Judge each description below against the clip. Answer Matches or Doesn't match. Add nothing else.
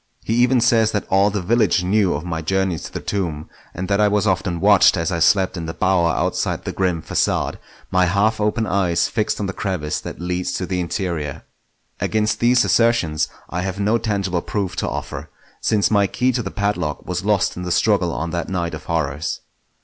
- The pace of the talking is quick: Matches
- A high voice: Doesn't match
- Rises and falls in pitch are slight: Doesn't match